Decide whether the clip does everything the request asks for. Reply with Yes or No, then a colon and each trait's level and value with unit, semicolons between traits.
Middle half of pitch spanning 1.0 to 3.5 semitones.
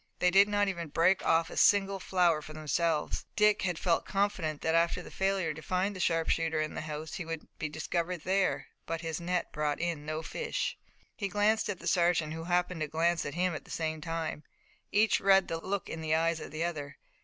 Yes: average, 2.8 semitones